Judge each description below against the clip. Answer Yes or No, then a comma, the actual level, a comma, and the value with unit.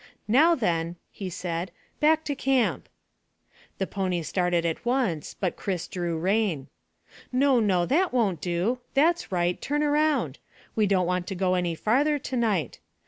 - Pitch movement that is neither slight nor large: No, wide, 7.0 semitones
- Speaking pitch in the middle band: No, high, 195 Hz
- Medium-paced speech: Yes, average, 155 wpm